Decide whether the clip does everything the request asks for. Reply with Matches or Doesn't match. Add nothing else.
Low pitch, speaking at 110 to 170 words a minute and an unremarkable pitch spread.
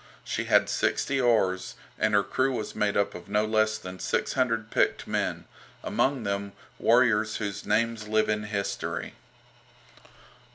Doesn't match